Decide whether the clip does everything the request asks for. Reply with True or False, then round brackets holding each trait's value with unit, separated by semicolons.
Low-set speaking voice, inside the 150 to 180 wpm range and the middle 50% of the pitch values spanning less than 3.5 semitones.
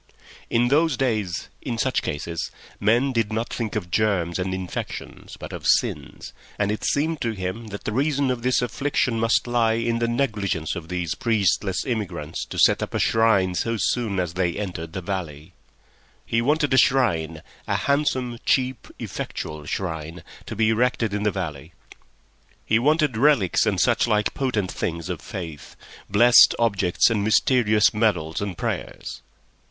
False (110 Hz; 160 wpm; 4.9 semitones)